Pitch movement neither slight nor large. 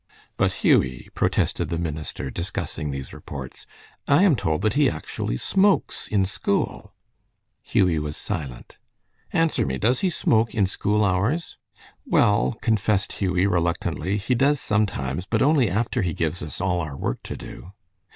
No: wide, 5.9 semitones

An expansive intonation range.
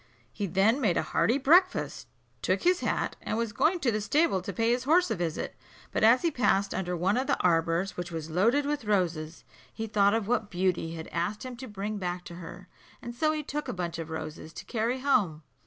Yes: wide, 6.3 semitones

